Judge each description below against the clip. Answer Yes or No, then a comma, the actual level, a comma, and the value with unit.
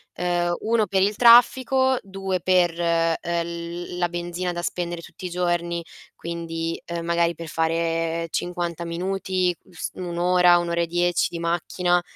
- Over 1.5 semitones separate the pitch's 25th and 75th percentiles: No, narrow, 1.2 semitones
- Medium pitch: Yes, medium, 175 Hz